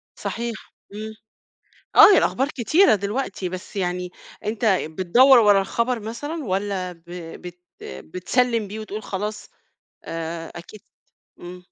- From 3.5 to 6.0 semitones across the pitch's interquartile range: Yes, average, 4.4 semitones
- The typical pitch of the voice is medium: No, high, 205 Hz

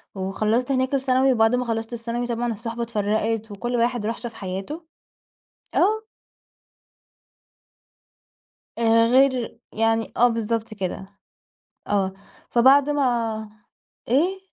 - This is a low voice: No, high, 230 Hz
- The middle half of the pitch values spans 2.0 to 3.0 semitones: Yes, narrow, 2.5 semitones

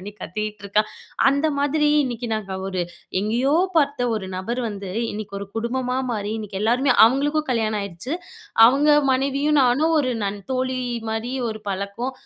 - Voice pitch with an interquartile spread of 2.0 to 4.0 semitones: No, average, 4.5 semitones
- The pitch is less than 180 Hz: No, high, 240 Hz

